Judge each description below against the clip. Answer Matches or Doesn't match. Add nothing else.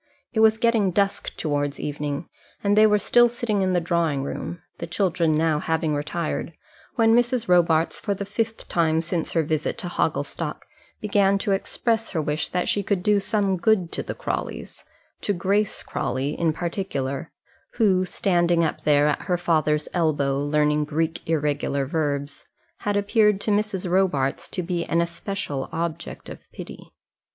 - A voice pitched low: Doesn't match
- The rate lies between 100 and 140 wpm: Doesn't match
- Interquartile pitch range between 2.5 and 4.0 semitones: Doesn't match